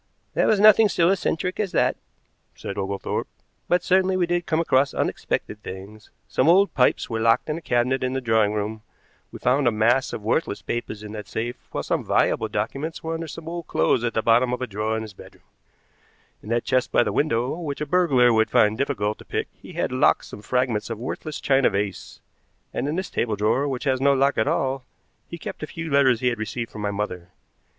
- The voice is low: Yes, low, 125 Hz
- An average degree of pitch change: No, wide, 5.9 semitones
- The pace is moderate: No, fast, 220 wpm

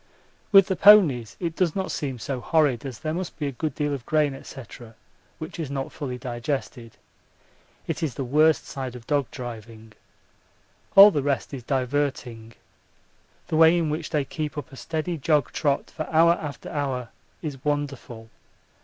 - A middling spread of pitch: Yes, average, 3.8 semitones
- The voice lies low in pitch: No, medium, 145 Hz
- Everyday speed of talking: Yes, average, 170 wpm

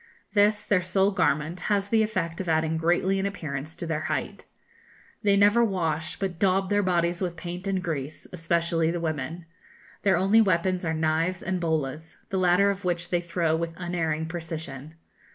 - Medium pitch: Yes, medium, 175 Hz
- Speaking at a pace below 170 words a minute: No, average, 175 wpm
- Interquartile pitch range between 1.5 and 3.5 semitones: Yes, average, 3.0 semitones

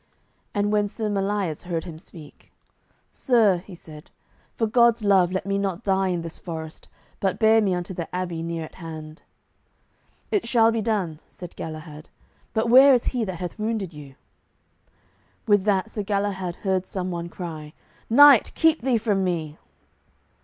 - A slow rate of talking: No, average, 165 wpm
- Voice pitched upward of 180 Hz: Yes, high, 190 Hz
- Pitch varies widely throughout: No, average, 4.3 semitones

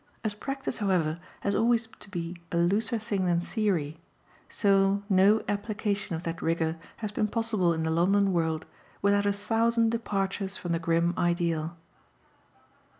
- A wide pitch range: No, average, 3.8 semitones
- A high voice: Yes, high, 195 Hz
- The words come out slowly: No, average, 150 wpm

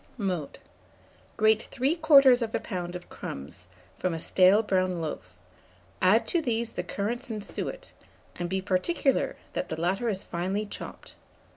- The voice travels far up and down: No, average, 4.8 semitones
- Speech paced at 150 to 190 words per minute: No, average, 140 wpm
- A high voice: Yes, high, 200 Hz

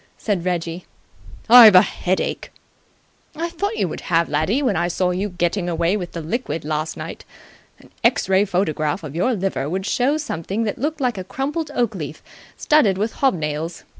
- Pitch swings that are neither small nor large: No, wide, 6.0 semitones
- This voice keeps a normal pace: Yes, average, 185 wpm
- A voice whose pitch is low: No, medium, 185 Hz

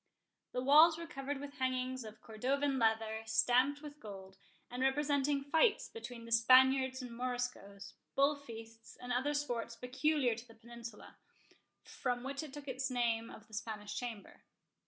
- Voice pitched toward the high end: Yes, very high, 250 Hz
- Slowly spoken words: No, average, 155 wpm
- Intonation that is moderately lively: Yes, average, 3.6 semitones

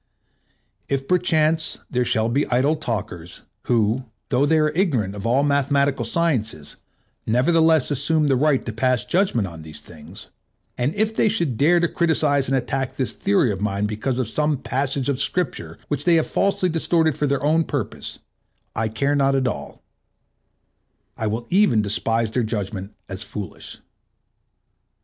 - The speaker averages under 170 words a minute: Yes, average, 160 wpm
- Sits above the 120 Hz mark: Yes, low, 135 Hz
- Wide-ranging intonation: Yes, wide, 5.7 semitones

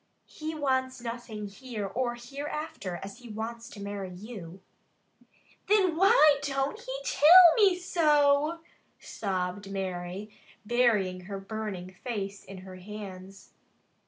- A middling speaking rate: No, slow, 120 wpm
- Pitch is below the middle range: No, high, 220 Hz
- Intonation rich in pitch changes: Yes, wide, 6.4 semitones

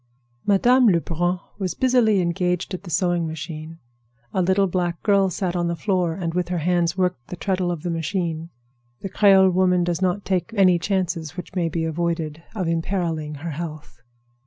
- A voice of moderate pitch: Yes, medium, 175 Hz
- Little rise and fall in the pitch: Yes, narrow, 2.2 semitones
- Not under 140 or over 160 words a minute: No, average, 180 wpm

